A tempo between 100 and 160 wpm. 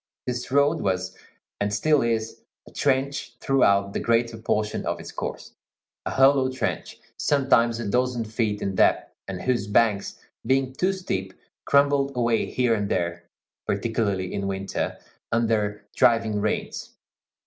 Yes: average, 140 wpm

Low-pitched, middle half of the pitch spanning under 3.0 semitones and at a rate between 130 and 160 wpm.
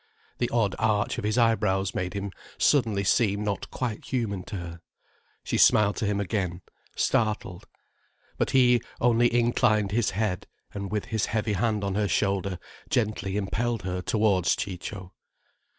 Yes: low, 105 Hz; narrow, 2.6 semitones; average, 150 wpm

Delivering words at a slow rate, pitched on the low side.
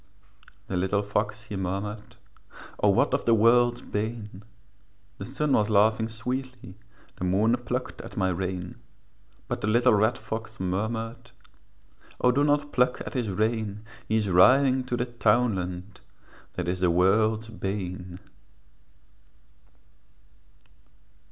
Yes: slow, 130 wpm; low, 110 Hz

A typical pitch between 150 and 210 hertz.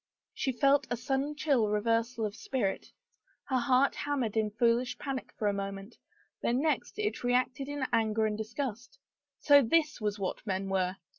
No: high, 240 Hz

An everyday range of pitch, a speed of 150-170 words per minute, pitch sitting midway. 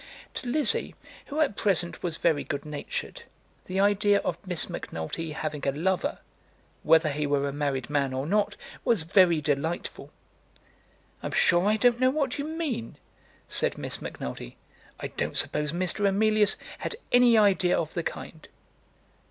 No: wide, 6.1 semitones; average, 155 wpm; medium, 175 Hz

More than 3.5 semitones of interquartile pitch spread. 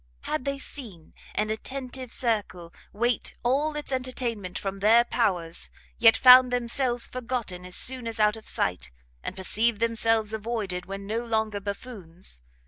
Yes: average, 3.9 semitones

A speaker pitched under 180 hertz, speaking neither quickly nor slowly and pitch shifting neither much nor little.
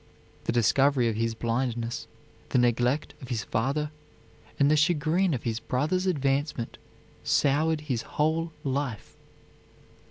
No: low, 135 Hz; slow, 125 wpm; average, 4.2 semitones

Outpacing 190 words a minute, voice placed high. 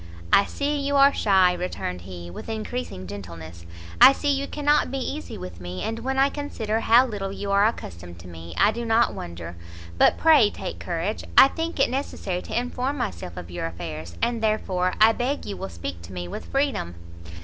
Yes: average, 200 wpm; high, 200 Hz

